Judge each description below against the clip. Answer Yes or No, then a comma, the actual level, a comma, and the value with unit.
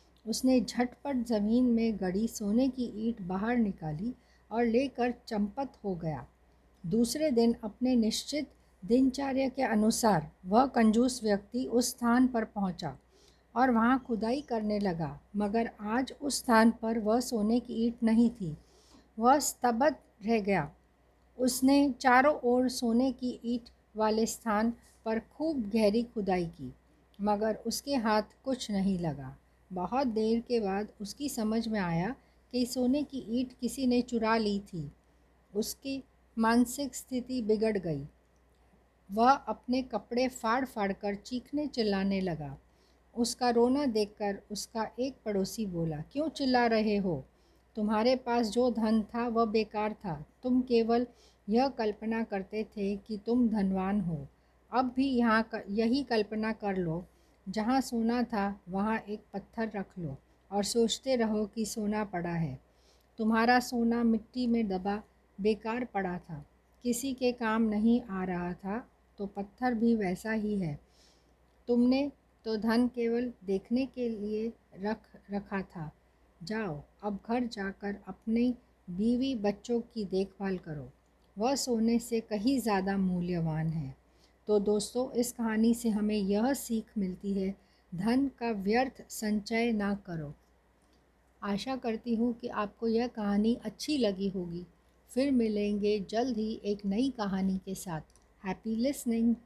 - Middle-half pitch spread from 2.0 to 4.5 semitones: Yes, average, 3.3 semitones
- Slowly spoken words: No, average, 140 wpm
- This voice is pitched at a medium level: No, high, 220 Hz